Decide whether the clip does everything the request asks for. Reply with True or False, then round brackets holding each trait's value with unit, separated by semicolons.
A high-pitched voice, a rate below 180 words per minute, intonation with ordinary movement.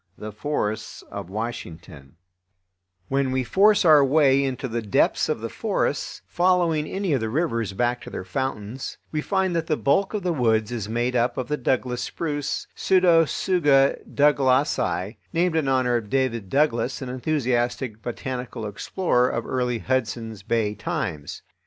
False (130 Hz; 155 wpm; 4.7 semitones)